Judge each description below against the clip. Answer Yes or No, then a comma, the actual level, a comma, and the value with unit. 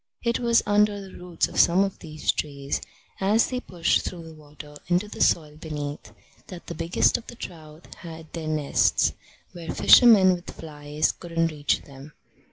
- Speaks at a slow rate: No, average, 175 wpm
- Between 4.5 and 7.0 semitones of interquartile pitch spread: No, average, 3.8 semitones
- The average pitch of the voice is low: No, medium, 165 Hz